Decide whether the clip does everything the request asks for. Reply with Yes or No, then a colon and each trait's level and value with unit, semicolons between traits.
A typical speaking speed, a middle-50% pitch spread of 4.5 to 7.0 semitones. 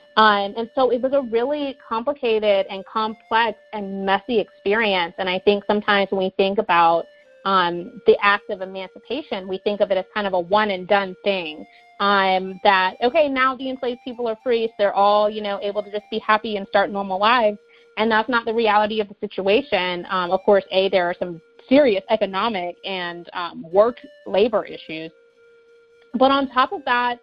No: average, 195 wpm; average, 3.5 semitones